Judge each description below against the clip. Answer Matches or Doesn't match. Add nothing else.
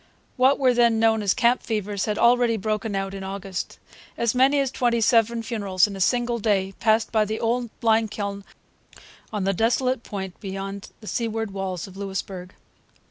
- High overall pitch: Matches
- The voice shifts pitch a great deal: Doesn't match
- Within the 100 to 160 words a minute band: Doesn't match